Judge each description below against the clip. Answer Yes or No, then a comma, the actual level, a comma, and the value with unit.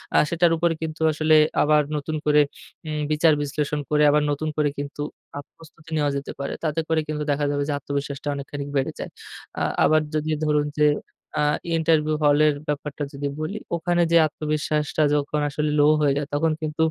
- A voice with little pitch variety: Yes, narrow, 1.3 semitones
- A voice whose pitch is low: No, medium, 150 Hz